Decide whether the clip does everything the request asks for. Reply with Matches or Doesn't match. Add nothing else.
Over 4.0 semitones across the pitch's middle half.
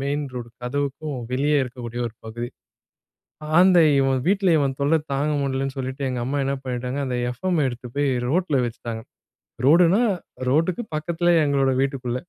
Doesn't match